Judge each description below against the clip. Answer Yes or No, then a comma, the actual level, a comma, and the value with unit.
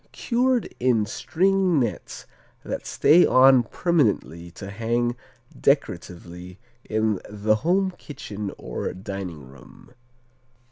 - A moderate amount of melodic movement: No, wide, 7.9 semitones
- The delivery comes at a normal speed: No, slow, 100 wpm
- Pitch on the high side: No, low, 115 Hz